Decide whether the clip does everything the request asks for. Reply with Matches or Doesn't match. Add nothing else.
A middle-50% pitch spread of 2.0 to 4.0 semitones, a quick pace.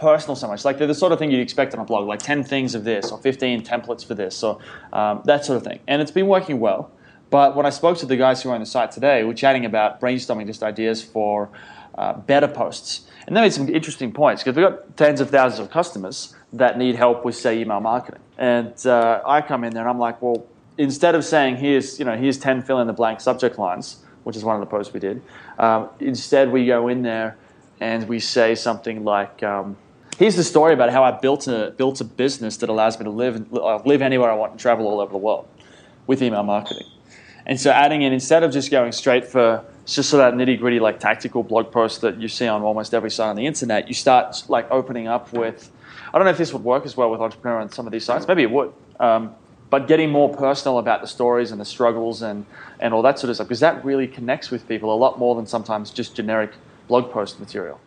Matches